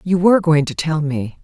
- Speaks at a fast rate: Yes, fast, 250 wpm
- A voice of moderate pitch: Yes, medium, 160 Hz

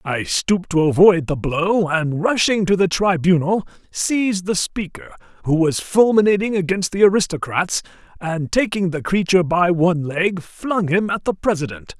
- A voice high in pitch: No, medium, 180 Hz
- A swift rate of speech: No, average, 160 wpm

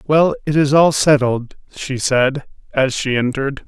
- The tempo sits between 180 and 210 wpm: No, average, 165 wpm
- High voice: No, medium, 140 Hz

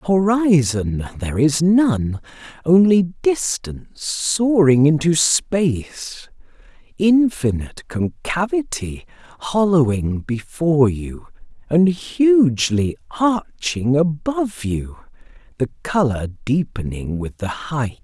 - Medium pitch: Yes, medium, 150 Hz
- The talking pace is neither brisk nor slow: No, slow, 75 wpm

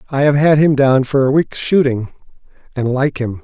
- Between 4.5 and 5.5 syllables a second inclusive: Yes, 5.1 syllables/s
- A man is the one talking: Yes, male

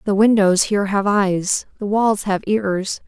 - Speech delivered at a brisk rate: No, average, 175 wpm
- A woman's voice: Yes, female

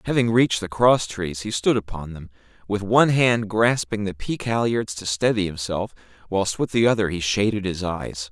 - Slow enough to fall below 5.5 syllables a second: Yes, 5.0 syllables/s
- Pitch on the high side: No, low, 105 Hz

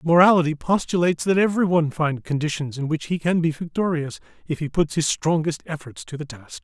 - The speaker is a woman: No, male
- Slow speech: No, average, 190 wpm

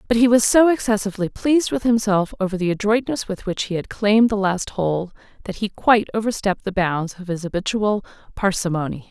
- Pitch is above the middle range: Yes, high, 205 Hz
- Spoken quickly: No, average, 190 wpm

